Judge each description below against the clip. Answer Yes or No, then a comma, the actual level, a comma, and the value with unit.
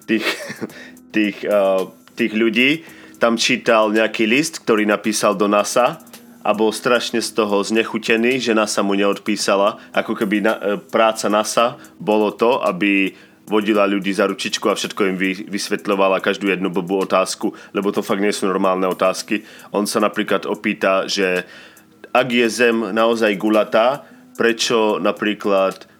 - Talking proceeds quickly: No, average, 145 wpm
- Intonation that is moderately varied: No, narrow, 2.3 semitones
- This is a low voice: Yes, low, 105 Hz